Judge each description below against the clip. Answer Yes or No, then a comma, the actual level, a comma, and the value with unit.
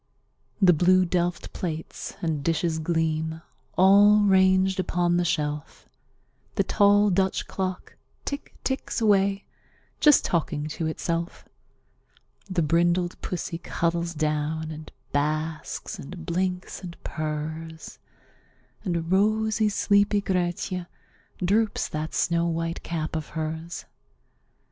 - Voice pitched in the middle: Yes, medium, 170 Hz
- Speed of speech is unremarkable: No, slow, 110 wpm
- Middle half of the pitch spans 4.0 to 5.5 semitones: No, average, 3.0 semitones